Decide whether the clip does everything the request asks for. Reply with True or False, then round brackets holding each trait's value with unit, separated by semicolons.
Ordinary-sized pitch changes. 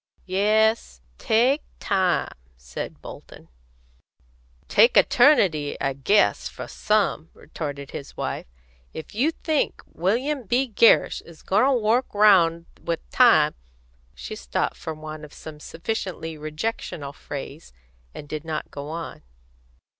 False (6.5 semitones)